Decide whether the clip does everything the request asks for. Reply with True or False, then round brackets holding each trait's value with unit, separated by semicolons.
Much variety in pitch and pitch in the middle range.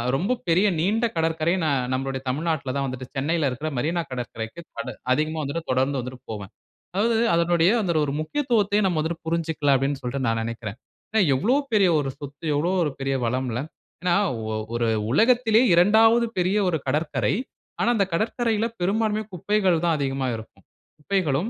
True (6.5 semitones; 160 Hz)